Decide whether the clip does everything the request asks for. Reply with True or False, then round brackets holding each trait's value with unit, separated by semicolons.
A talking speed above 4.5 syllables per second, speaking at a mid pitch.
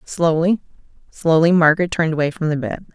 True (6.1 syllables/s; 165 Hz)